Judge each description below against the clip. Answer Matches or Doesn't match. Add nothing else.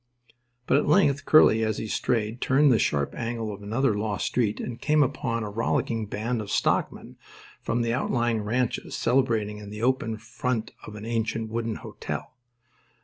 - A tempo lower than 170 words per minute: Doesn't match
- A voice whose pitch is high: Doesn't match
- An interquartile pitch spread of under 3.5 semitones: Matches